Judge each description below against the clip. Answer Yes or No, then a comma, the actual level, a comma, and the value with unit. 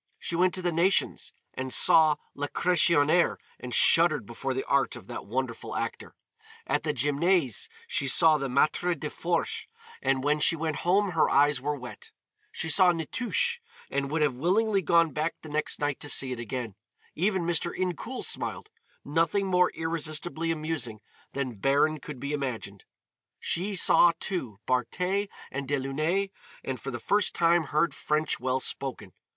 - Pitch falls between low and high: Yes, medium, 155 Hz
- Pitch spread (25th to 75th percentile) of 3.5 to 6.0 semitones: Yes, average, 4.3 semitones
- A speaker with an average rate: Yes, average, 160 wpm